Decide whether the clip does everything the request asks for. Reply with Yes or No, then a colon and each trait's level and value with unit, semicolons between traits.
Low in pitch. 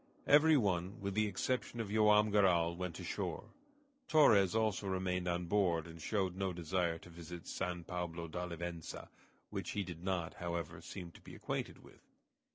Yes: very low, 90 Hz